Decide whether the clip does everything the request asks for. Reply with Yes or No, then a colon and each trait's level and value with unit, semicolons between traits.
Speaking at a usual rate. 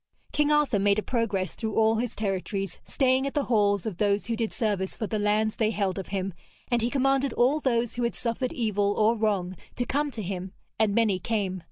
No: fast, 220 wpm